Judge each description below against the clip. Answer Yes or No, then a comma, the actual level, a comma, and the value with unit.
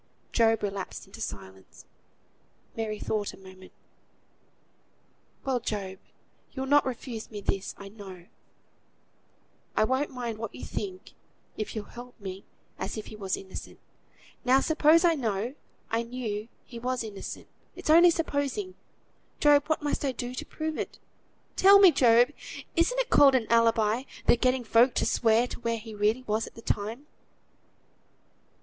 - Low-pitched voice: No, high, 235 Hz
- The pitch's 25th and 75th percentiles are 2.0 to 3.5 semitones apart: No, average, 4.3 semitones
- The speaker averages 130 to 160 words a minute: Yes, average, 155 wpm